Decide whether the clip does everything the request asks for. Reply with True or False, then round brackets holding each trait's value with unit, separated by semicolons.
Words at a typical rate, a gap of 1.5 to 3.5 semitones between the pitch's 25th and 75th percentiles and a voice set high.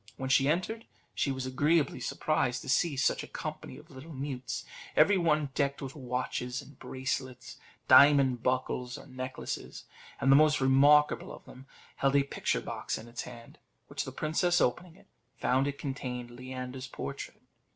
False (160 wpm; 2.5 semitones; 135 Hz)